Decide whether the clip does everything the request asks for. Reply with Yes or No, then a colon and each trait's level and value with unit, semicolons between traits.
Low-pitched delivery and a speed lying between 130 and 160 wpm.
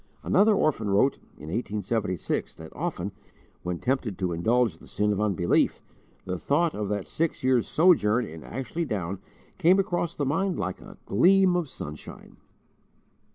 Yes: low, 115 Hz; average, 155 wpm